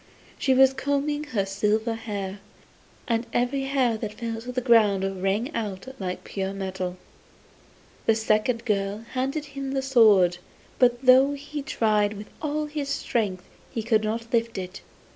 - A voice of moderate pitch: No, high, 230 Hz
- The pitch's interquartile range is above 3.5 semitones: Yes, average, 4.7 semitones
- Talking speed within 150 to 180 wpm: Yes, average, 155 wpm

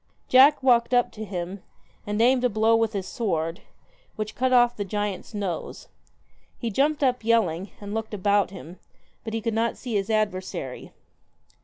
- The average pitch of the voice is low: No, high, 215 Hz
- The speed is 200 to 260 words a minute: No, average, 165 wpm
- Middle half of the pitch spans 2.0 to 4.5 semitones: Yes, average, 3.3 semitones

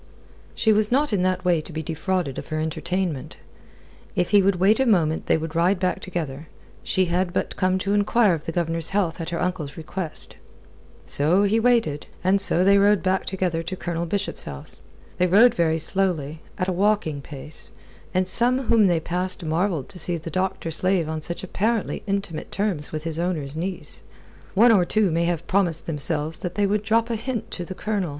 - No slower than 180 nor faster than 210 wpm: Yes, average, 200 wpm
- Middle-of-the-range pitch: Yes, medium, 180 Hz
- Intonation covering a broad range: No, average, 3.6 semitones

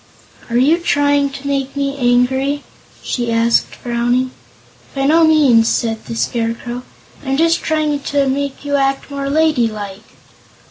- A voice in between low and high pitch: No, very high, 275 Hz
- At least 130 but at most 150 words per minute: Yes, average, 140 wpm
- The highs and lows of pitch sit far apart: No, average, 3.0 semitones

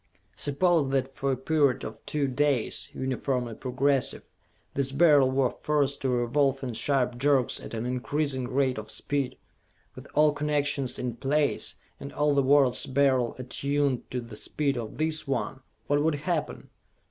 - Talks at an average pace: Yes, average, 160 wpm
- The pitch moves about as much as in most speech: No, narrow, 2.3 semitones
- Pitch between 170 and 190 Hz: No, low, 135 Hz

